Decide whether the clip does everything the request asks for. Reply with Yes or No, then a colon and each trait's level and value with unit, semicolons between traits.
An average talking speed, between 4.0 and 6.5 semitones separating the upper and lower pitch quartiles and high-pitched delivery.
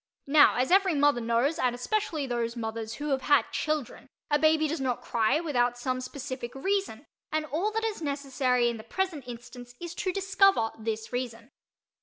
Yes: average, 180 wpm; average, 4.5 semitones; very high, 270 Hz